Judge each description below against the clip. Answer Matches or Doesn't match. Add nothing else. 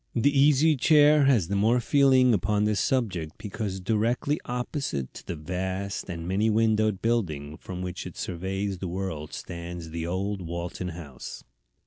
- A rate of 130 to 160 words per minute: Matches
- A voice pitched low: Matches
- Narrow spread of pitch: Doesn't match